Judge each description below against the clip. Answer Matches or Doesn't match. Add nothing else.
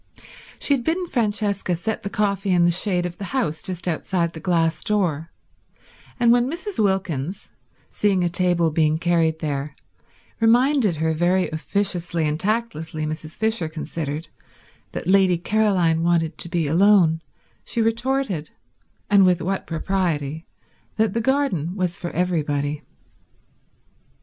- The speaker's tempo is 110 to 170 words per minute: Matches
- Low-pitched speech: Doesn't match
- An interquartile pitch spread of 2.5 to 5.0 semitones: Matches